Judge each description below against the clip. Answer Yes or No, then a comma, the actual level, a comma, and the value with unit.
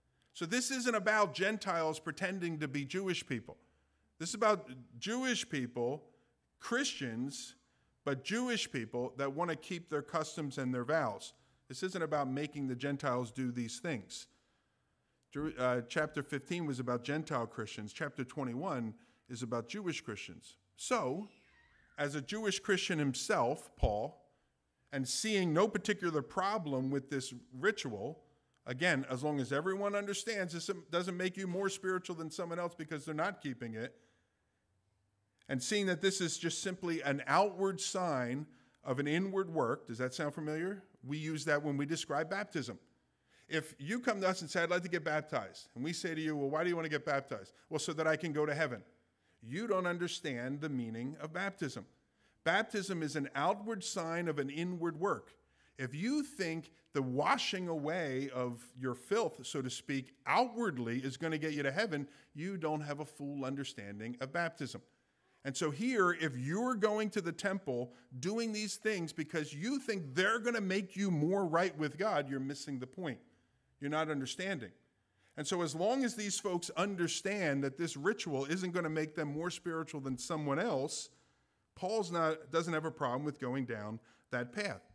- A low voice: No, medium, 155 Hz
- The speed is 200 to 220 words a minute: No, average, 175 wpm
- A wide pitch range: Yes, wide, 5.8 semitones